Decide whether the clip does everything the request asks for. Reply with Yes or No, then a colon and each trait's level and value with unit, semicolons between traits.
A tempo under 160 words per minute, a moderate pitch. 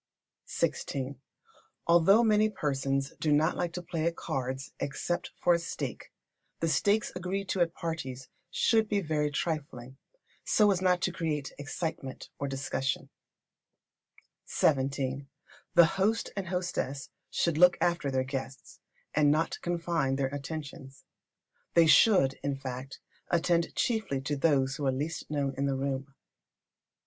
Yes: average, 140 wpm; medium, 150 Hz